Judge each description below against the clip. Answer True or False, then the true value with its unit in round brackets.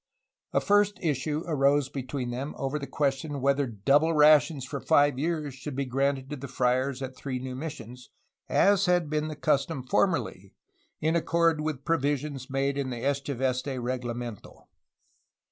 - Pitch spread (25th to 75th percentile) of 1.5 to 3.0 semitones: True (2.7 semitones)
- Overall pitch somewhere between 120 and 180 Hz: True (140 Hz)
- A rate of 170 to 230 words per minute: False (155 wpm)